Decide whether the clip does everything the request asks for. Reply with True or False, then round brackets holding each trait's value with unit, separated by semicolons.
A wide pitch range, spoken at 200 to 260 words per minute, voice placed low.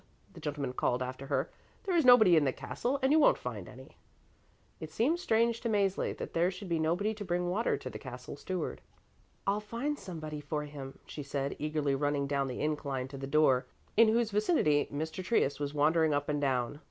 False (6.6 semitones; 205 wpm; 155 Hz)